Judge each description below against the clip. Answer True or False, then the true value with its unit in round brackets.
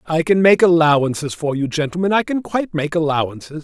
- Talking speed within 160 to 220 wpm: True (200 wpm)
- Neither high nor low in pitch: True (165 Hz)